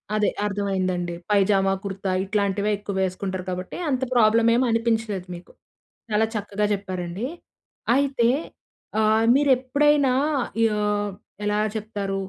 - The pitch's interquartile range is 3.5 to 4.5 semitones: No, average, 2.7 semitones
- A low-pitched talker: No, high, 205 Hz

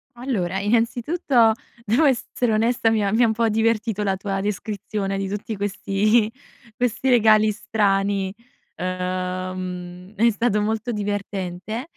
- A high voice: Yes, high, 210 Hz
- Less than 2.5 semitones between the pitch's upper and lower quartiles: No, average, 2.8 semitones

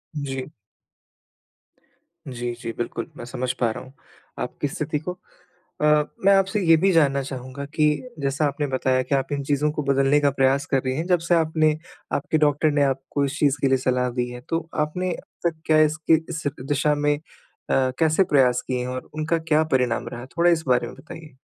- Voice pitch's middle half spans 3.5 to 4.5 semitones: No, average, 3.0 semitones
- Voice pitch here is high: No, medium, 145 Hz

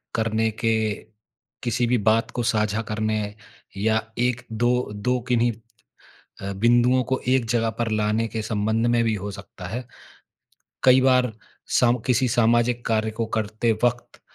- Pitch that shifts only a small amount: Yes, narrow, 1.9 semitones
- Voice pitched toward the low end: Yes, low, 115 Hz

